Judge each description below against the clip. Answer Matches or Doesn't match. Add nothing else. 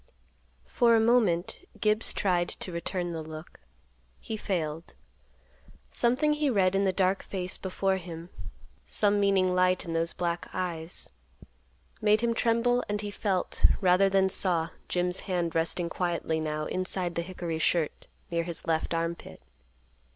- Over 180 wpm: Doesn't match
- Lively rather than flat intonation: Doesn't match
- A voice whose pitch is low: Doesn't match